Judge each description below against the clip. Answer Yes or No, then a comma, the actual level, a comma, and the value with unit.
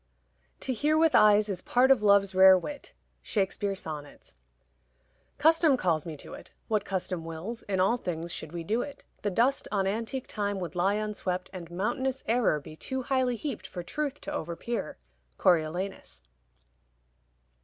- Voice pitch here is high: Yes, high, 200 Hz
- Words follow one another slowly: No, average, 155 wpm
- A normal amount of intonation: No, wide, 5.7 semitones